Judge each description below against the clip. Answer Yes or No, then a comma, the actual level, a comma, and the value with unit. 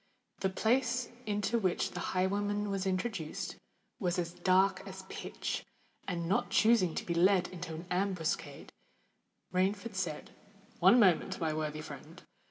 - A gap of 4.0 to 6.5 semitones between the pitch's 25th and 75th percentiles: No, average, 2.8 semitones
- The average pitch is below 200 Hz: Yes, medium, 185 Hz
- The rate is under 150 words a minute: Yes, average, 140 wpm